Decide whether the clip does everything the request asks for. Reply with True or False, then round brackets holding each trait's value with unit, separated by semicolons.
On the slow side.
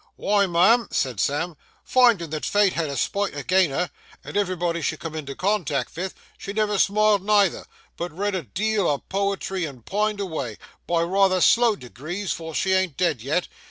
False (175 wpm)